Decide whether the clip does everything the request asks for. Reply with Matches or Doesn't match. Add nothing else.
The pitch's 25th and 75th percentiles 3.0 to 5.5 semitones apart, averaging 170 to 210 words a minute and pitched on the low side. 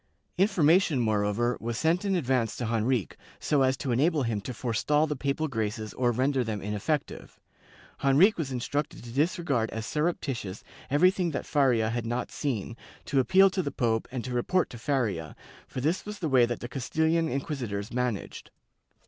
Matches